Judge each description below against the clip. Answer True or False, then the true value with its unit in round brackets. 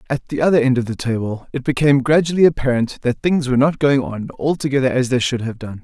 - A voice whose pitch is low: True (130 Hz)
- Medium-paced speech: False (235 wpm)